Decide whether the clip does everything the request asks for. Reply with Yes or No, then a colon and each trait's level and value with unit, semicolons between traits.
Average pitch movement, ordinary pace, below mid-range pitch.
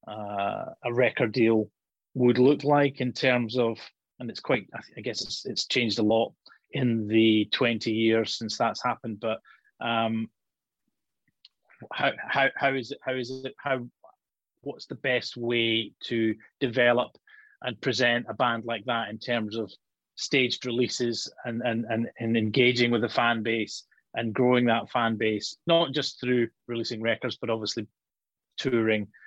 No: narrow, 2.0 semitones; average, 160 wpm; low, 120 Hz